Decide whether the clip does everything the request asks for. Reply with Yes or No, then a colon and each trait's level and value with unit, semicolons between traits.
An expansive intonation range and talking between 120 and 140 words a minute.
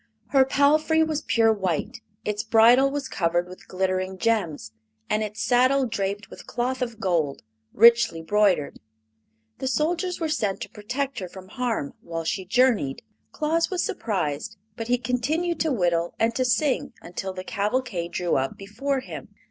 No: wide, 5.8 semitones; average, 160 wpm